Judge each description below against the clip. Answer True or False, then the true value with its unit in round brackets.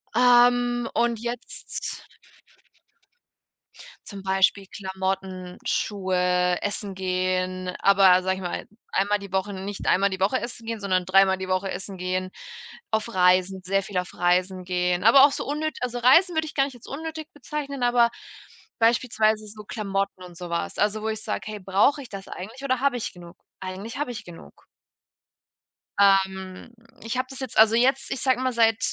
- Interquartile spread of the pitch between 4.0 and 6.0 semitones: True (4.5 semitones)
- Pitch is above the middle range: True (200 Hz)